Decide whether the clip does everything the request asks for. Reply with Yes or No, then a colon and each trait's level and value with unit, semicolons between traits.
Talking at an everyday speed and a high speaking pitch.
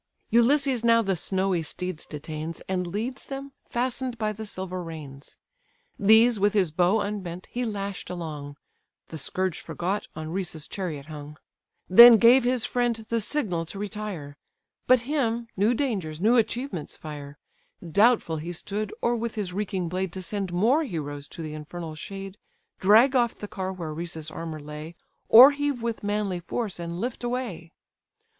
Yes: average, 160 wpm; high, 195 Hz